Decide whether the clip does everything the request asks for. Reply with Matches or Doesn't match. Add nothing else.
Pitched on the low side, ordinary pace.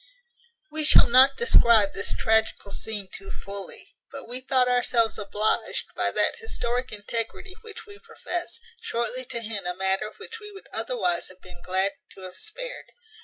Doesn't match